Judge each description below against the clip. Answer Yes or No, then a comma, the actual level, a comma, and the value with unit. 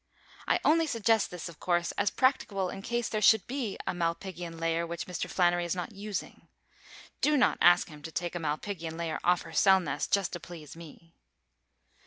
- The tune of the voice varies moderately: Yes, average, 3.3 semitones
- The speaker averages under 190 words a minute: No, average, 195 wpm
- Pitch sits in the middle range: Yes, medium, 175 Hz